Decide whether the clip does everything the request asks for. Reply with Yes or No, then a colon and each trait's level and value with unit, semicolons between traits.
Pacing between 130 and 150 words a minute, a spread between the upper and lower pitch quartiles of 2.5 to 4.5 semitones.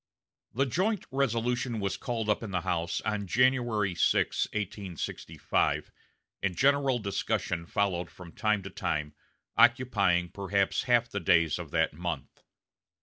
No: slow, 135 wpm; average, 5.2 semitones